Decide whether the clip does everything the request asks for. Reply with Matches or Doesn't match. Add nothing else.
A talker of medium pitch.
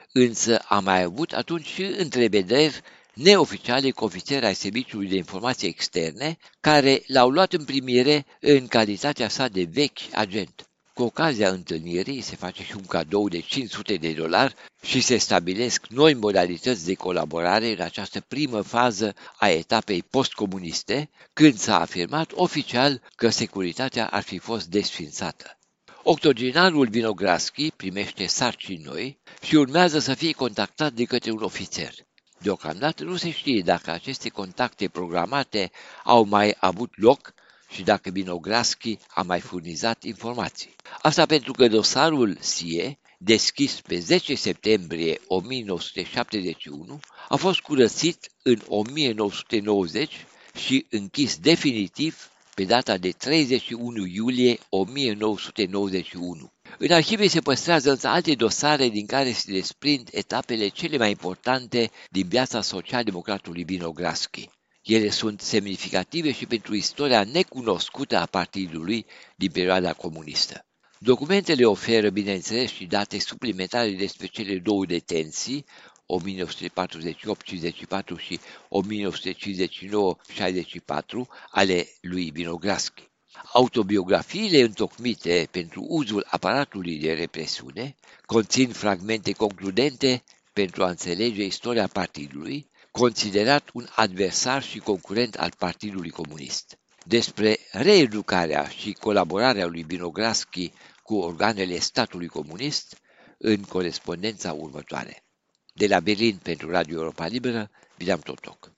Doesn't match